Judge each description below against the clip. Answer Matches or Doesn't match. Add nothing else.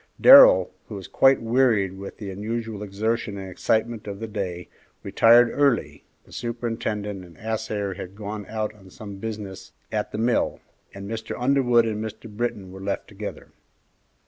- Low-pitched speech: Matches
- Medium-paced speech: Matches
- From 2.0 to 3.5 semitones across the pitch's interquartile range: Matches